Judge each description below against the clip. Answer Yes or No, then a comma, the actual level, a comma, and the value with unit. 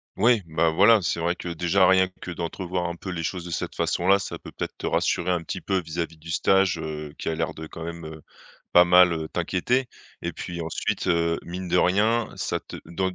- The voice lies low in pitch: Yes, very low, 85 Hz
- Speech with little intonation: Yes, narrow, 2.2 semitones